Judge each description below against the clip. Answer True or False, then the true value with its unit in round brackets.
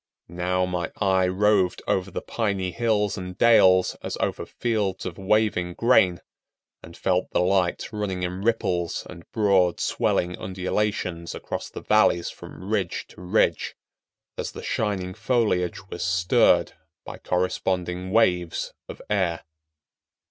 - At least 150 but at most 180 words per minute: False (135 wpm)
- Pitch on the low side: True (95 Hz)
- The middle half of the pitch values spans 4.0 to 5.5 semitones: False (2.5 semitones)